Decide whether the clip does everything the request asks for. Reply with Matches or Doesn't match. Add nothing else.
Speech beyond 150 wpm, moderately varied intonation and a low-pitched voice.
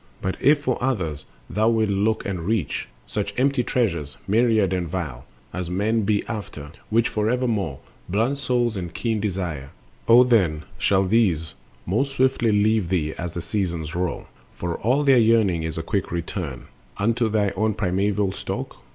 Matches